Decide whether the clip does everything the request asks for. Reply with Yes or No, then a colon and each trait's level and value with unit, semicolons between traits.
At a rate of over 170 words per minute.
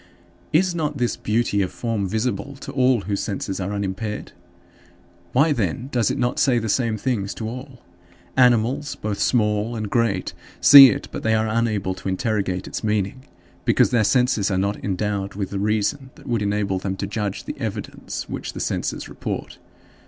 Yes: average, 180 wpm